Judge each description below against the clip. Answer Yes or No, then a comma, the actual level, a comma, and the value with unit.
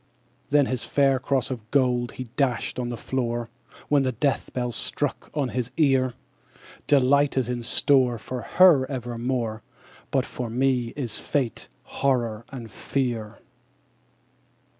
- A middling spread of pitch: No, narrow, 2.2 semitones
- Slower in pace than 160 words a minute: Yes, average, 145 wpm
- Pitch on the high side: No, low, 125 Hz